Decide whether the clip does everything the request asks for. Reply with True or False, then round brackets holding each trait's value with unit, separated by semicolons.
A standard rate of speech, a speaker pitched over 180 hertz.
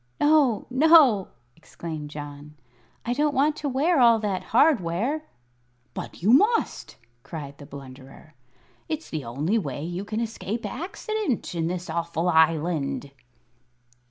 False (130 wpm; 190 Hz)